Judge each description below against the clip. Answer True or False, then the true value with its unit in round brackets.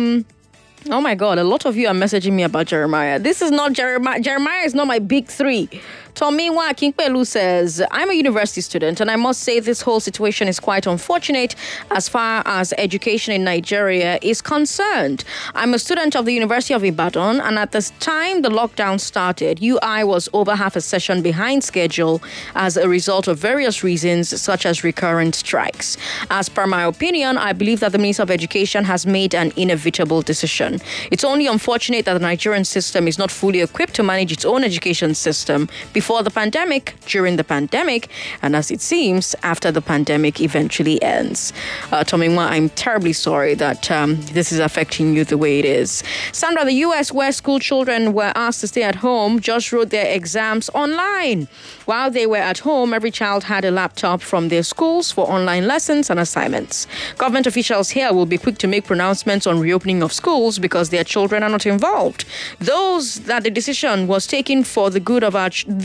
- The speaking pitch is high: True (205 Hz)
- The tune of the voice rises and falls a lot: True (5.7 semitones)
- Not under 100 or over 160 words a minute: False (190 wpm)